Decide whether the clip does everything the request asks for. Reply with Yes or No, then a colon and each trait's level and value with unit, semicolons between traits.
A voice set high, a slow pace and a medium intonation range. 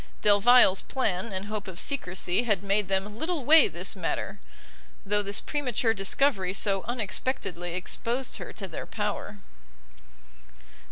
Yes: high, 205 Hz; slow, 130 wpm; average, 4.1 semitones